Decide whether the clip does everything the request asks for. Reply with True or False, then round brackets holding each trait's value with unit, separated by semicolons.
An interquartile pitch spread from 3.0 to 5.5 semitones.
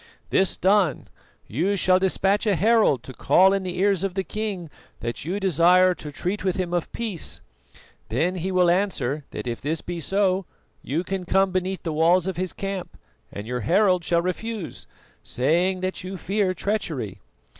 False (2.6 semitones)